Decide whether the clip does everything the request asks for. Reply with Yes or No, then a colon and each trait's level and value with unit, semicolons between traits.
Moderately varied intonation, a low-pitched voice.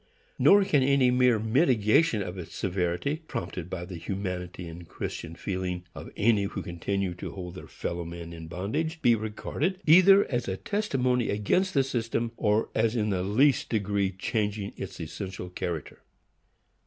No: wide, 5.7 semitones; low, 105 Hz